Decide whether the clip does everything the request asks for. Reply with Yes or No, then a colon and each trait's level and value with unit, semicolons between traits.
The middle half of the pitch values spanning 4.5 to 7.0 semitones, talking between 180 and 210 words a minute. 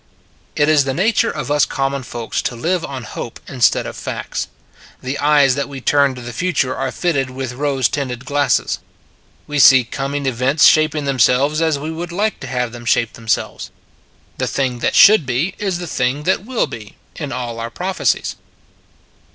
No: average, 3.4 semitones; average, 185 wpm